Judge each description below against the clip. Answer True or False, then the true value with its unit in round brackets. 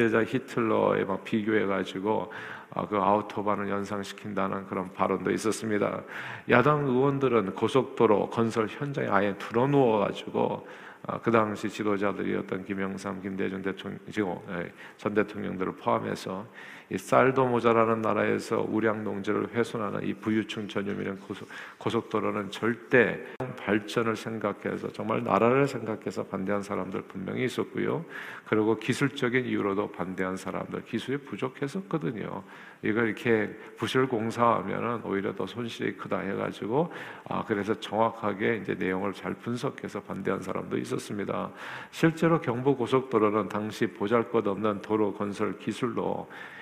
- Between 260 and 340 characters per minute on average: True (325 characters per minute)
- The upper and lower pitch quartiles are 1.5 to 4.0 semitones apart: True (2.8 semitones)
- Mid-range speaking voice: False (105 Hz)